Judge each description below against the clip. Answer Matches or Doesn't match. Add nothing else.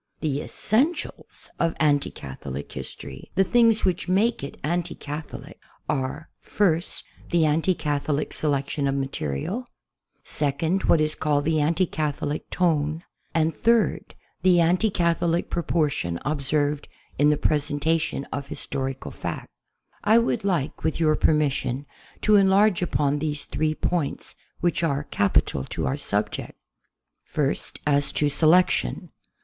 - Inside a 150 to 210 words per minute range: Doesn't match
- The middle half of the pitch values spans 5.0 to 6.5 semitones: Doesn't match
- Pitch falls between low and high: Matches